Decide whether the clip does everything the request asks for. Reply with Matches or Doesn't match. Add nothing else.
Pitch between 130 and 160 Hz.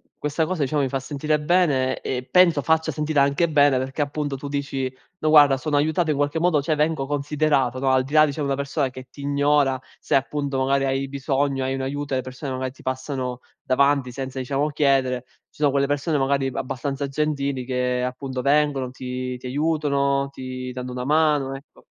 Matches